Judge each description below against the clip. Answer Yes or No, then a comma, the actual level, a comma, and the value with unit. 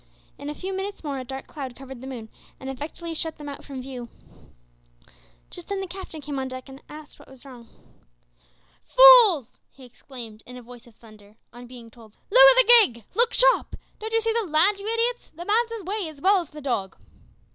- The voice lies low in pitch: No, very high, 290 Hz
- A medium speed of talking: No, fast, 210 wpm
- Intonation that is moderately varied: No, wide, 7.8 semitones